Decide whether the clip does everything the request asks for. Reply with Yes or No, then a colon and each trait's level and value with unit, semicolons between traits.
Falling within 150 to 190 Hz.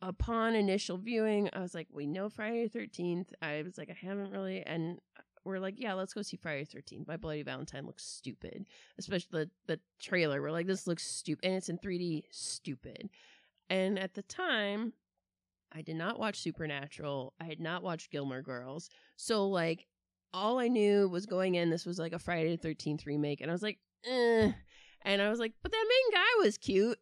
Yes: medium, 185 Hz